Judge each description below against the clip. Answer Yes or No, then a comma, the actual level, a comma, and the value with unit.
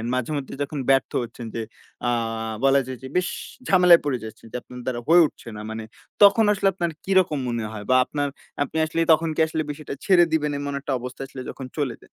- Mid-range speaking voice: Yes, medium, 145 Hz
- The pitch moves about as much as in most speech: Yes, average, 4.6 semitones